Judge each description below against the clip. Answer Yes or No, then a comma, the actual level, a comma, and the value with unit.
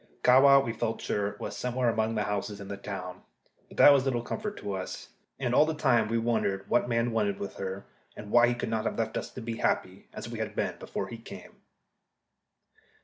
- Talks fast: Yes, fast, 220 wpm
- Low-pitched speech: Yes, low, 115 Hz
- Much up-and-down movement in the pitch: No, average, 3.1 semitones